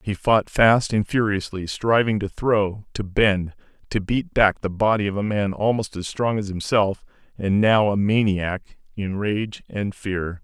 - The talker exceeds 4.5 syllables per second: No, 4.0 syllables/s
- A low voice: Yes, low, 105 Hz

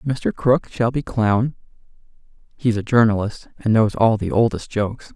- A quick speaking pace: No, average, 165 wpm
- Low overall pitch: Yes, low, 115 Hz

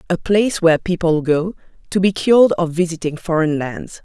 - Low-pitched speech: No, medium, 170 Hz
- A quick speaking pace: No, average, 180 wpm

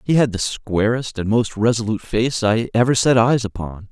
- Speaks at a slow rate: No, average, 200 wpm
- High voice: No, low, 115 Hz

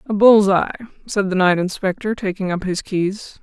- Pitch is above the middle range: Yes, high, 195 Hz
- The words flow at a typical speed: Yes, average, 195 wpm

